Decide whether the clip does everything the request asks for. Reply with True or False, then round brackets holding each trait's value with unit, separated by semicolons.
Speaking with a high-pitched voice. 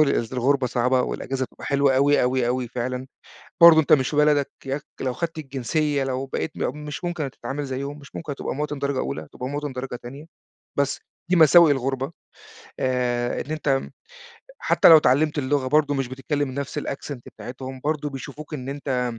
False (135 Hz)